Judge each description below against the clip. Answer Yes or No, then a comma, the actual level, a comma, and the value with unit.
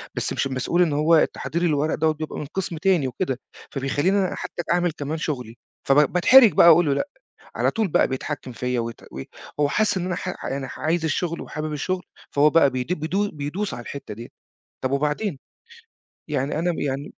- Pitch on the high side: No, medium, 155 Hz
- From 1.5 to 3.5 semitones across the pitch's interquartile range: No, average, 4.2 semitones